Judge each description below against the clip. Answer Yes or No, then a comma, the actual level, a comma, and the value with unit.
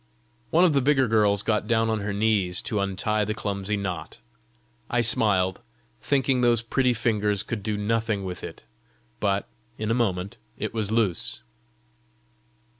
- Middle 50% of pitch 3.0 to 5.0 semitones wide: No, narrow, 2.6 semitones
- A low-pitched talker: Yes, low, 105 Hz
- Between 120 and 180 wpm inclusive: Yes, average, 155 wpm